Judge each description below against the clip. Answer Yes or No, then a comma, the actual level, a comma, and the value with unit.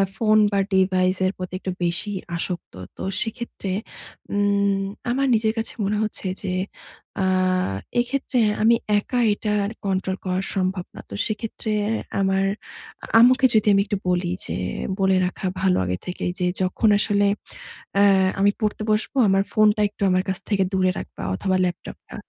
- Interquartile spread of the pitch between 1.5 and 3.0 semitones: Yes, narrow, 2.4 semitones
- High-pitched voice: Yes, high, 195 Hz